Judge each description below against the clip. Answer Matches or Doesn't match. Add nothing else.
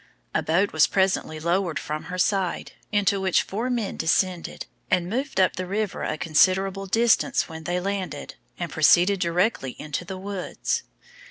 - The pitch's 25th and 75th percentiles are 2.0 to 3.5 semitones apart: Matches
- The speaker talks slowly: Doesn't match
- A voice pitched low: Doesn't match